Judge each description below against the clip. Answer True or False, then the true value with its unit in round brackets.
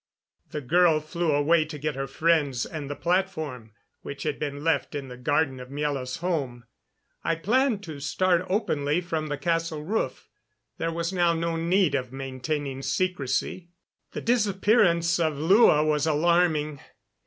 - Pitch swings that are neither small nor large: True (3.4 semitones)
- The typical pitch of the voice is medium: True (155 Hz)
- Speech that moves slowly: False (155 wpm)